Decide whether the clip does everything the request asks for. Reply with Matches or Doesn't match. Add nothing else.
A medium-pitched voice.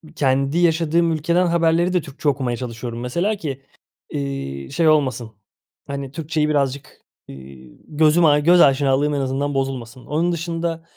Matches